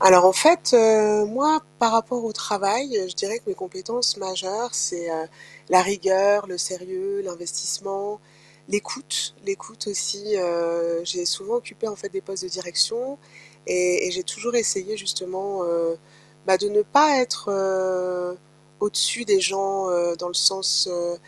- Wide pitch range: No, average, 3.4 semitones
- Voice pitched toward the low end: No, high, 195 Hz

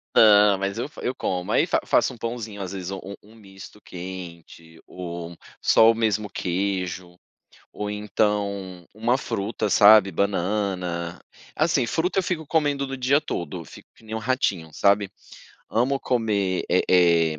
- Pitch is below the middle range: Yes, low, 100 Hz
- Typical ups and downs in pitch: Yes, average, 3.7 semitones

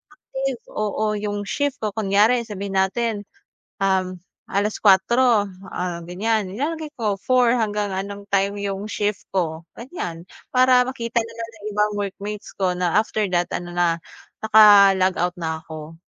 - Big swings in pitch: No, average, 3.0 semitones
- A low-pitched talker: No, high, 205 Hz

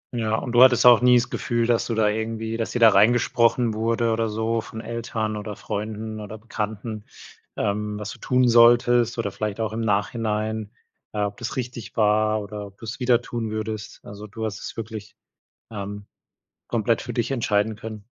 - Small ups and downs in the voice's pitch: Yes, narrow, 1.7 semitones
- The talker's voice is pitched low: Yes, low, 110 Hz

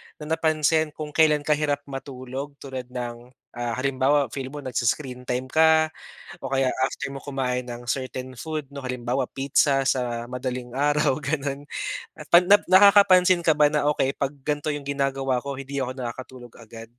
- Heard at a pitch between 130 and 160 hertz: Yes, low, 135 Hz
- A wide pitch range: No, narrow, 2.6 semitones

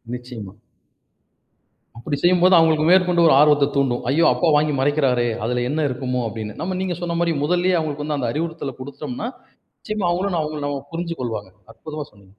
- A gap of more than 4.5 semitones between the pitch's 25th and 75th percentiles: Yes, average, 5.1 semitones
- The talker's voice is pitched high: No, medium, 150 Hz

